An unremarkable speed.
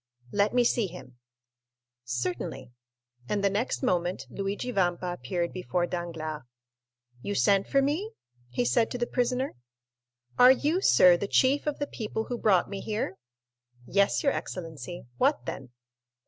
Yes: average, 145 wpm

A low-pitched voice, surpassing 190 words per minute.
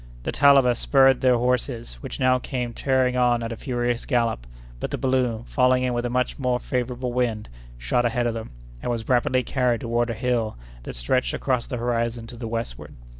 Yes: low, 120 Hz; average, 200 wpm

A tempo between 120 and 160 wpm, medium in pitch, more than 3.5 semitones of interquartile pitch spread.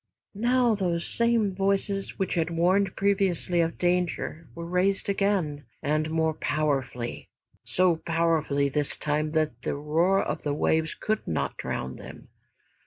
Yes: average, 140 wpm; medium, 170 Hz; average, 4.2 semitones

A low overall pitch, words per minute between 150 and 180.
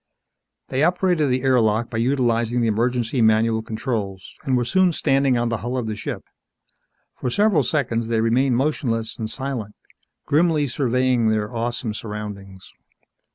Yes: low, 120 Hz; average, 155 wpm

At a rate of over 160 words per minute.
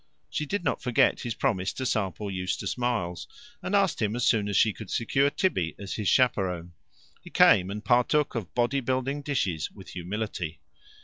Yes: average, 180 wpm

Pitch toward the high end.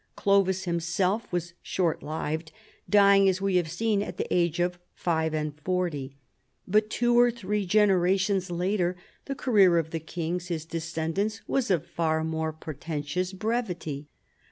No: medium, 180 Hz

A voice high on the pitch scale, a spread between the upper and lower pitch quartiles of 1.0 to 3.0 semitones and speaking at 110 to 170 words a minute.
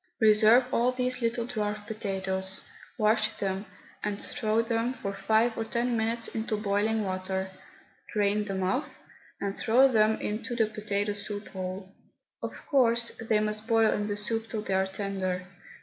Yes: high, 215 Hz; narrow, 2.4 semitones; average, 160 wpm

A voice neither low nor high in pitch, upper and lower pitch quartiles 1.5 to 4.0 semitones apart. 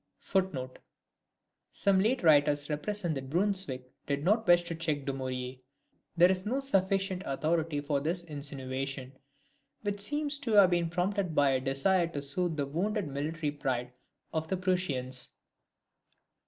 No: medium, 165 Hz; average, 5.2 semitones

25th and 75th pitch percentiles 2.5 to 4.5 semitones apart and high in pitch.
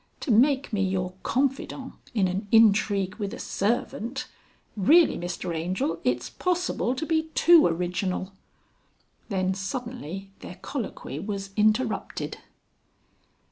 No: wide, 5.6 semitones; high, 205 Hz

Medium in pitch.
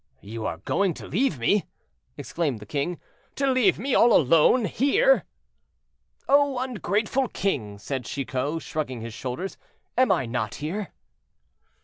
Yes: medium, 165 Hz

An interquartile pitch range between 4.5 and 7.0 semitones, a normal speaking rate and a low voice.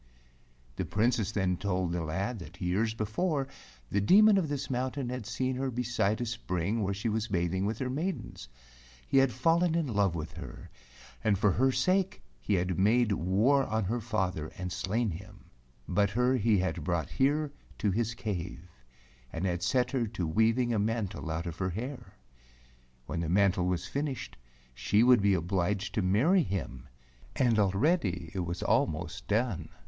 Yes: average, 5.2 semitones; average, 175 wpm; low, 105 Hz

